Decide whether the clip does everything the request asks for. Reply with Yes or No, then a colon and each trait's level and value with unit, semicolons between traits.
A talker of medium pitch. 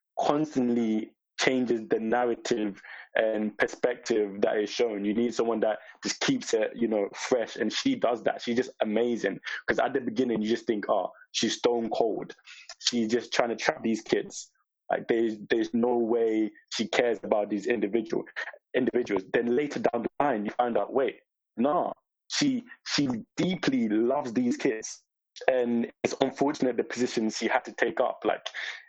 No: low, 120 Hz